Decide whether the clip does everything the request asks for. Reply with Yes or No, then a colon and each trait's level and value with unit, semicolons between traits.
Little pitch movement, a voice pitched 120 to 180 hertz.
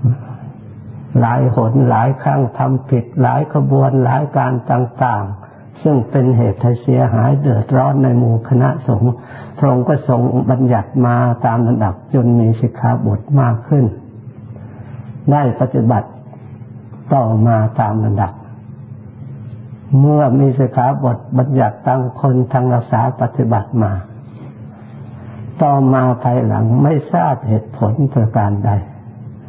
Yes: narrow, 2.2 semitones; low, 125 Hz